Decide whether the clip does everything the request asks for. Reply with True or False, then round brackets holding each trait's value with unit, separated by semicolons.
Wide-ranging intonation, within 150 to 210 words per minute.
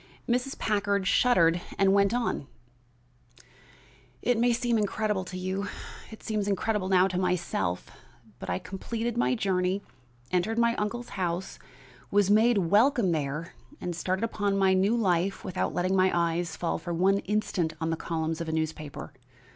False (3.7 semitones; 155 wpm)